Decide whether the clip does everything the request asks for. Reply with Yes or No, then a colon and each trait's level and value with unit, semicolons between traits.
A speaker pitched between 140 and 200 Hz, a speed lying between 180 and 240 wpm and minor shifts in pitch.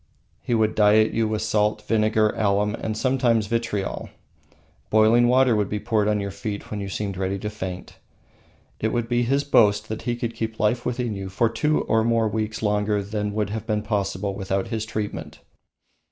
No: low, 110 Hz; average, 190 wpm; narrow, 1.8 semitones